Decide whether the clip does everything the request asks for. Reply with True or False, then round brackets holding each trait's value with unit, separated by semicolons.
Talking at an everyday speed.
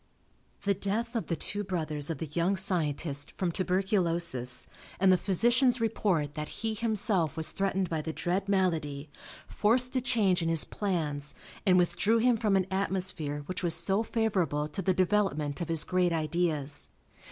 True (165 wpm)